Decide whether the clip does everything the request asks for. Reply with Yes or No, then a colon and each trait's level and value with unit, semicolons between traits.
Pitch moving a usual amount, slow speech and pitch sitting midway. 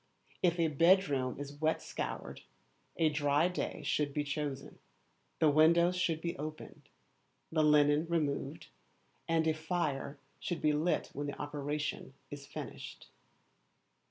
No: narrow, 2.3 semitones; slow, 130 wpm; medium, 150 Hz